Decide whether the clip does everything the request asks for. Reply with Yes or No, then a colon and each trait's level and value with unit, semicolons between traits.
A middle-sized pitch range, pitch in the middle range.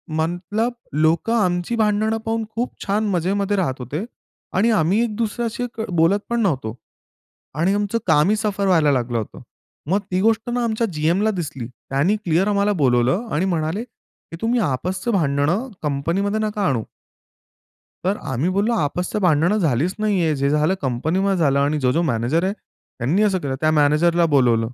No: wide, 6.0 semitones; medium, 180 Hz